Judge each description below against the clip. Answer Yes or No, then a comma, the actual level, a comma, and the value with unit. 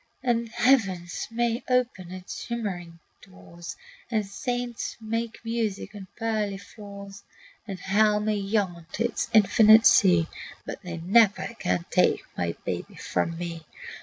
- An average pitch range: Yes, average, 4.0 semitones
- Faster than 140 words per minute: No, slow, 135 wpm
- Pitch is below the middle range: No, high, 205 Hz